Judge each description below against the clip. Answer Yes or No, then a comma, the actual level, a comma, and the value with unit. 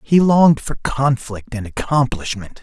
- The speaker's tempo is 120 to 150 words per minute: Yes, slow, 135 wpm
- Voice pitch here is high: No, low, 130 Hz